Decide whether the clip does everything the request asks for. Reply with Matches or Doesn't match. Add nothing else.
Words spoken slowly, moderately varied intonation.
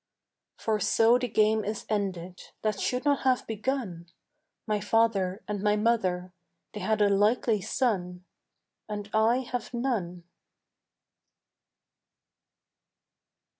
Matches